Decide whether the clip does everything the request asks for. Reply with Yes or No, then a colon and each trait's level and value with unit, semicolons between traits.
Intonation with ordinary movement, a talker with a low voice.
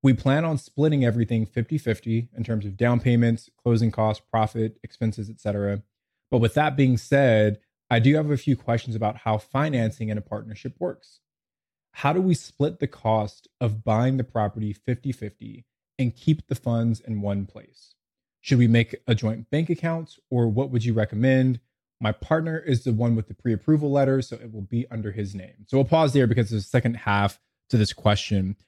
Yes: average, 3.6 semitones; low, 115 Hz